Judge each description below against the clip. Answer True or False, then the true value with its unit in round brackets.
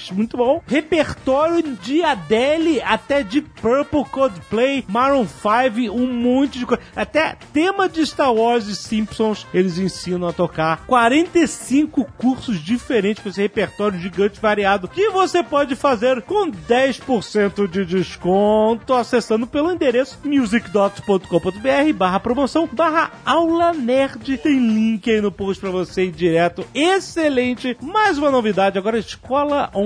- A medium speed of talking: True (135 wpm)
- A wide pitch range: True (5.7 semitones)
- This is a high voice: True (245 Hz)